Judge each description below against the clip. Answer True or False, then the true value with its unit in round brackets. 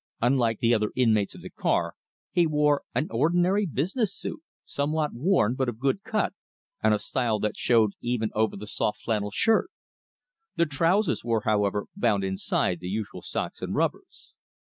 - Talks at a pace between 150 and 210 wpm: True (165 wpm)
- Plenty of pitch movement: True (6.8 semitones)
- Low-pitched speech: True (120 Hz)